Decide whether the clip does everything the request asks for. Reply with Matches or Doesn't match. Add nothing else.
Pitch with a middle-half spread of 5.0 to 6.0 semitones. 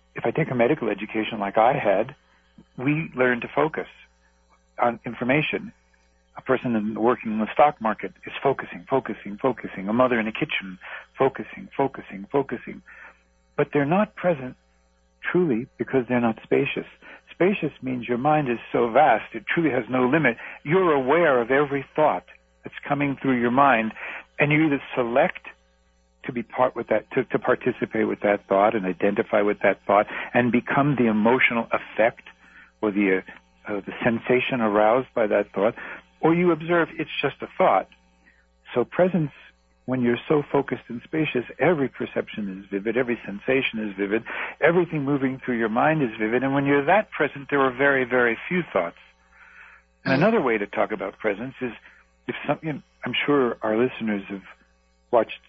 Matches